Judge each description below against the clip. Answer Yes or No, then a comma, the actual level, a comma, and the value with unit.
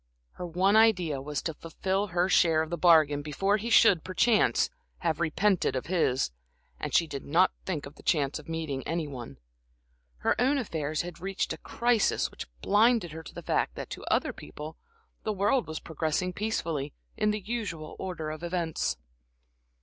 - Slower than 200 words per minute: Yes, average, 180 wpm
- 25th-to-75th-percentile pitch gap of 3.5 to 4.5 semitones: Yes, average, 4.1 semitones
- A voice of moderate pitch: Yes, medium, 170 Hz